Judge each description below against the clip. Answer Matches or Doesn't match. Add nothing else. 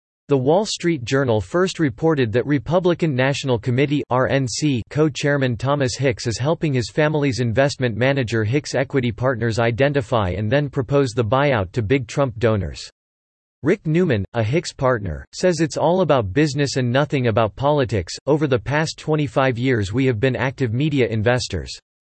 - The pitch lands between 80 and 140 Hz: Matches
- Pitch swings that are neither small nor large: Matches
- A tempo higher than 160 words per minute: Doesn't match